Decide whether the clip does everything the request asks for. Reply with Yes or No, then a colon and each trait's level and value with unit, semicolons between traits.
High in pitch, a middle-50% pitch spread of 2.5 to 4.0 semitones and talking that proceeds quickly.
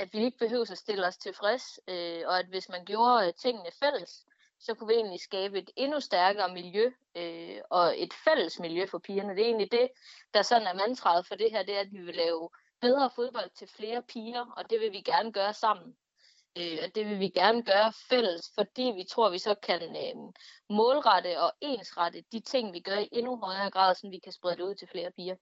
No: high, 205 Hz; average, 4.4 semitones; fast, 230 wpm